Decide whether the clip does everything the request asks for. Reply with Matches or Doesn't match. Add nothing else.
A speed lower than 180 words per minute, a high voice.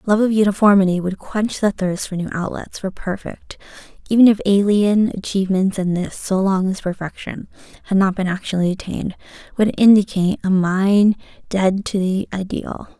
Matches